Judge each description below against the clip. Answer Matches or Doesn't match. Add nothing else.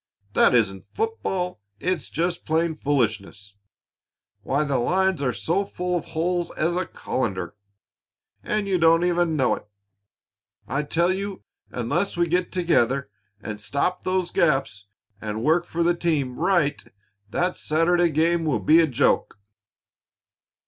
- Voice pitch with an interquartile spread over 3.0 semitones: Matches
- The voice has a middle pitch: Matches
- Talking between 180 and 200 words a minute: Doesn't match